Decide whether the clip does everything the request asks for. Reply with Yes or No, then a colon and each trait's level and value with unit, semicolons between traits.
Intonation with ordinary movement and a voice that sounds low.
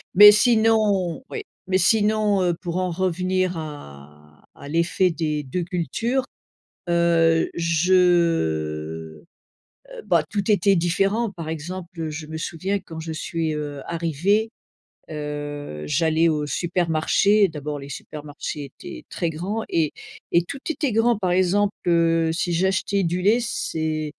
No: average, 3.9 semitones; medium, 170 Hz